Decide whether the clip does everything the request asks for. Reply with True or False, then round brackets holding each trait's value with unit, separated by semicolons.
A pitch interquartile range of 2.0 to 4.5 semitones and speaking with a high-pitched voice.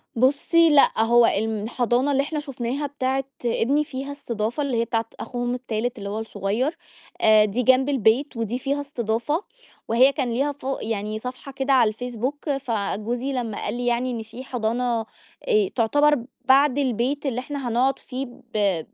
True (3.4 semitones; 250 Hz)